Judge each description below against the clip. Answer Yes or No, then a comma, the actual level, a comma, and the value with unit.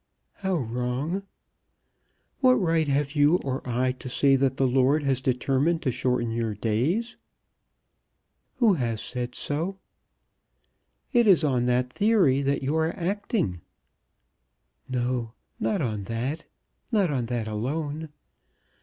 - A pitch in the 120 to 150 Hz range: Yes, low, 135 Hz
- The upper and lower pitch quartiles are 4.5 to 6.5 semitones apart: Yes, average, 5.0 semitones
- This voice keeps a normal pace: No, slow, 125 wpm